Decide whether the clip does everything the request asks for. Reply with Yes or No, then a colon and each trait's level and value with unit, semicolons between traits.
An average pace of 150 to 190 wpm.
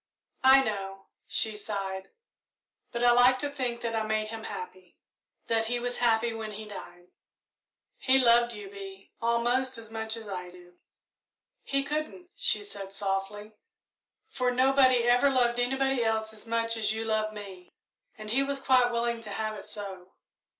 Yes: average, 165 wpm